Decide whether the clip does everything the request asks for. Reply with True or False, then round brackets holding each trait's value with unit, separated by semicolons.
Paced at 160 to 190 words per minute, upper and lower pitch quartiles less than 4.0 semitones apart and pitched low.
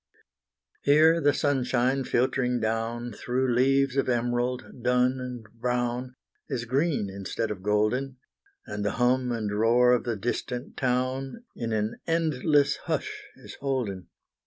False (135 wpm; 2.4 semitones; 125 Hz)